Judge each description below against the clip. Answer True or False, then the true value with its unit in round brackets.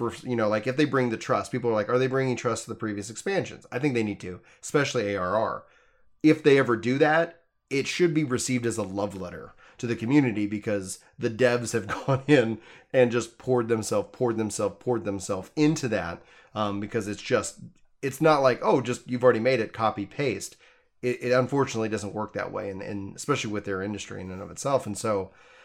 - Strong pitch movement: False (3.5 semitones)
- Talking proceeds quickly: True (215 wpm)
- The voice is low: True (120 Hz)